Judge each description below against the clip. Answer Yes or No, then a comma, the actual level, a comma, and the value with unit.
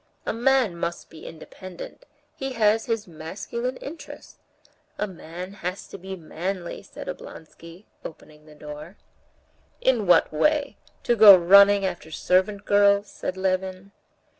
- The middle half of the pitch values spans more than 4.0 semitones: No, average, 3.7 semitones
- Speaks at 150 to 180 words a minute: No, slow, 135 wpm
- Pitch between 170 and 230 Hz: Yes, high, 190 Hz